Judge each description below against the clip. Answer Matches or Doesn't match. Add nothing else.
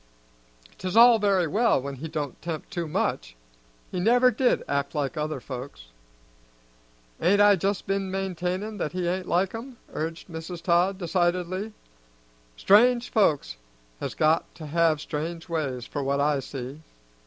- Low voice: Doesn't match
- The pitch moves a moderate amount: Matches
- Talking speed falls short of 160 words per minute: Matches